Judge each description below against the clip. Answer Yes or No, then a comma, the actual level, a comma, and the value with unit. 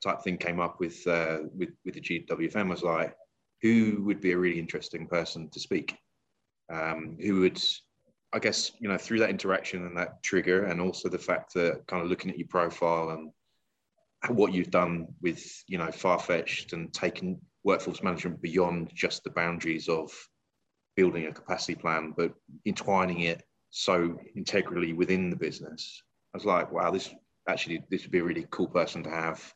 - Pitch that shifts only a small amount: Yes, narrow, 1.7 semitones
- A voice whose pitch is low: Yes, very low, 85 Hz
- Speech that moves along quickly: No, average, 185 wpm